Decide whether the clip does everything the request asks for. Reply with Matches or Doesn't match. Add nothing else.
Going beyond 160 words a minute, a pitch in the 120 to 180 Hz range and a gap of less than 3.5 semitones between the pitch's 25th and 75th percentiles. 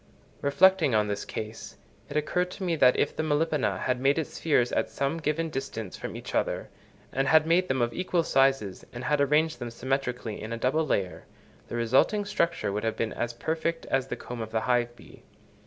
Doesn't match